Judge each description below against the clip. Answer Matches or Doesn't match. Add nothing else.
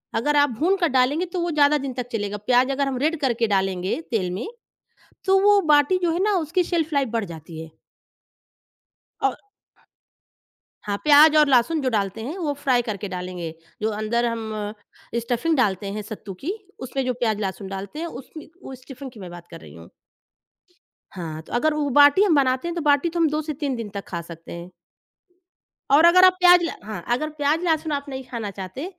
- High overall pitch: Matches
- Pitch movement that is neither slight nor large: Doesn't match